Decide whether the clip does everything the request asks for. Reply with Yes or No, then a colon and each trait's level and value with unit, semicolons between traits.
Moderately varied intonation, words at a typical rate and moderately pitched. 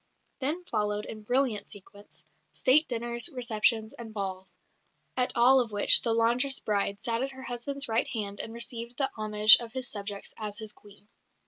No: average, 3.1 semitones; average, 175 wpm; high, 230 Hz